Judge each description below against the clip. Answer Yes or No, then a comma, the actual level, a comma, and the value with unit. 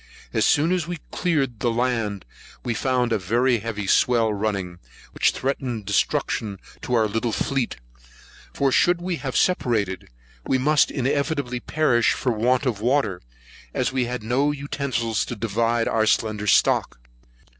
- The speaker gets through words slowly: No, average, 150 wpm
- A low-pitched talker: Yes, low, 120 Hz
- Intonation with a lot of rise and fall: No, average, 3.8 semitones